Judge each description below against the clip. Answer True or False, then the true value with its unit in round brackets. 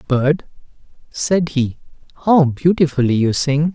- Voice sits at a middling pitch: True (150 Hz)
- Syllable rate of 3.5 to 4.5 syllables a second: True (4.0 syllables/s)